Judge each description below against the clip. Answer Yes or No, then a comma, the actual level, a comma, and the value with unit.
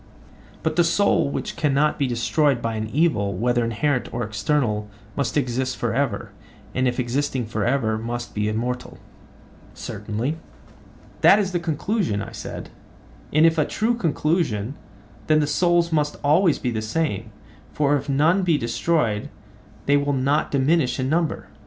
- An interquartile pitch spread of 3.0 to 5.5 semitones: Yes, average, 5.1 semitones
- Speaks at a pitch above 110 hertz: Yes, medium, 140 Hz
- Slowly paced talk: No, average, 160 wpm